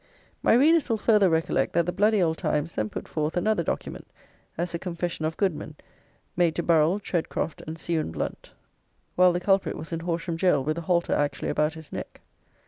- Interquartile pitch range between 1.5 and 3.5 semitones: Yes, narrow, 2.5 semitones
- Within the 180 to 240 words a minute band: Yes, average, 195 wpm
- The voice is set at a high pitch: No, medium, 170 Hz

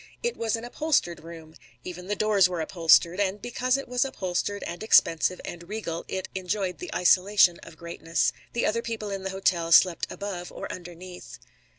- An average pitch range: Yes, average, 3.7 semitones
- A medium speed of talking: Yes, average, 180 wpm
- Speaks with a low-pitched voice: No, medium, 185 Hz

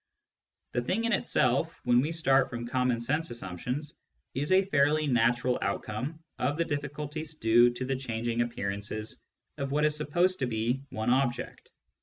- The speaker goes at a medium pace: Yes, average, 160 wpm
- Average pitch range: Yes, average, 4.1 semitones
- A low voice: Yes, low, 130 Hz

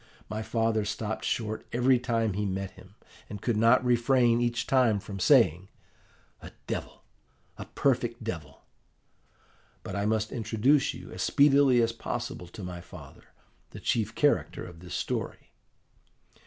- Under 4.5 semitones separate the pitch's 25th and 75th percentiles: Yes, average, 3.2 semitones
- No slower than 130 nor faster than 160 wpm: Yes, average, 145 wpm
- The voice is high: No, low, 110 Hz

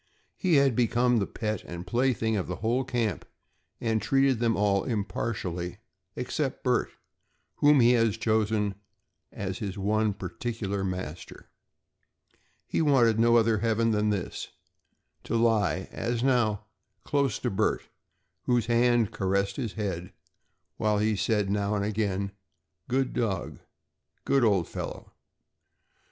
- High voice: No, low, 110 Hz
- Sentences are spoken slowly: Yes, slow, 130 wpm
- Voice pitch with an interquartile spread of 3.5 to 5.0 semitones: No, average, 3.0 semitones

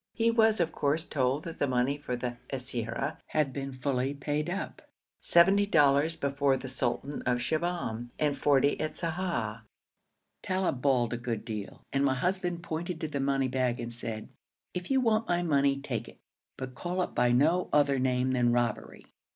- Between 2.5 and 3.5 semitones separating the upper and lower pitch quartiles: No, average, 4.9 semitones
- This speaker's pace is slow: No, average, 185 wpm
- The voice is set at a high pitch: No, medium, 140 Hz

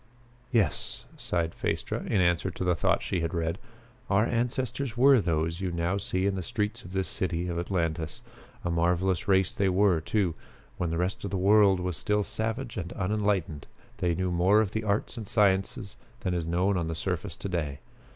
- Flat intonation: No, average, 3.2 semitones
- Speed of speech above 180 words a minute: Yes, average, 195 wpm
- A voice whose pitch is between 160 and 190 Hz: No, very low, 95 Hz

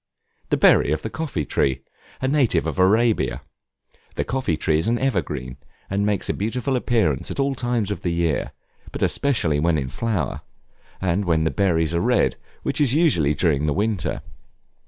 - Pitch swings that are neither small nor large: No, wide, 7.4 semitones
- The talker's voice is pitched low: Yes, very low, 95 Hz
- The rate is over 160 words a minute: Yes, average, 175 wpm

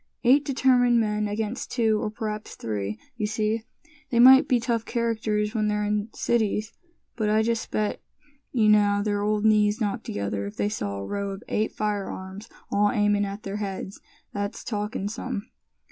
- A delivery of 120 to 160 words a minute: No, average, 175 wpm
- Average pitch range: No, narrow, 1.7 semitones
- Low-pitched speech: No, high, 210 Hz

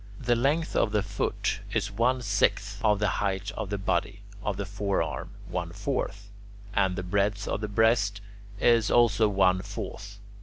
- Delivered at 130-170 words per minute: Yes, average, 165 wpm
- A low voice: Yes, low, 100 Hz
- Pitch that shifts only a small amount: Yes, narrow, 2.0 semitones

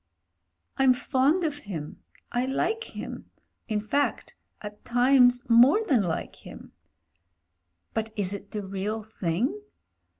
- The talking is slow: Yes, slow, 130 wpm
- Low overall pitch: No, high, 240 Hz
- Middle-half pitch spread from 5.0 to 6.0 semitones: No, average, 4.5 semitones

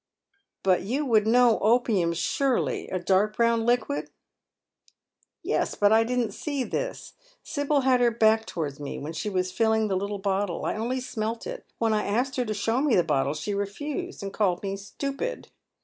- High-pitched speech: Yes, high, 220 Hz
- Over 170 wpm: Yes, average, 195 wpm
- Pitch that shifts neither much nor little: Yes, average, 4.2 semitones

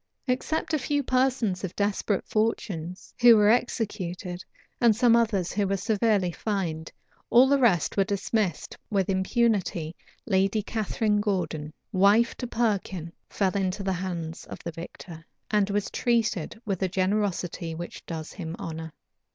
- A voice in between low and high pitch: No, high, 200 Hz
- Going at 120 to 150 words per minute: Yes, average, 145 wpm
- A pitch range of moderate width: Yes, average, 3.9 semitones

